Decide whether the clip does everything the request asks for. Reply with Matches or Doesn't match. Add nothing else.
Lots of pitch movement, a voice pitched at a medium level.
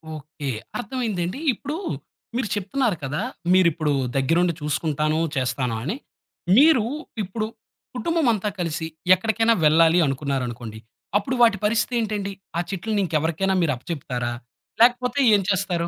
Matches